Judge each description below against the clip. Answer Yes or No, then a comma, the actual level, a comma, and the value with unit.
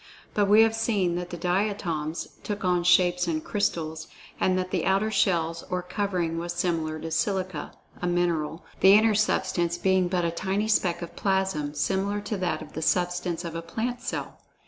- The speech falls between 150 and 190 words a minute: Yes, average, 185 wpm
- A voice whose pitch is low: No, medium, 180 Hz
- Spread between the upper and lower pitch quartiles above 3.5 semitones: No, average, 2.8 semitones